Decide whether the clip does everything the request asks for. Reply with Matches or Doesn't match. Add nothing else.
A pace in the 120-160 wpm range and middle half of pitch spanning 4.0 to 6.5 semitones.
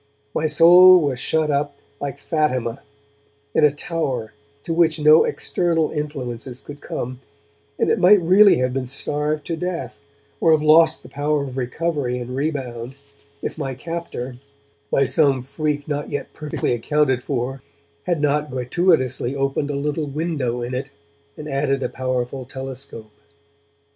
Doesn't match